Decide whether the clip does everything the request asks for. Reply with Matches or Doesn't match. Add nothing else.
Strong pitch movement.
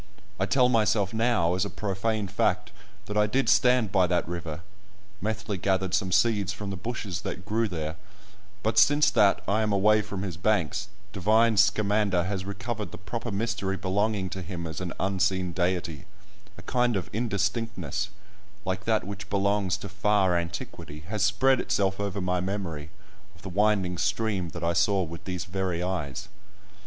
Doesn't match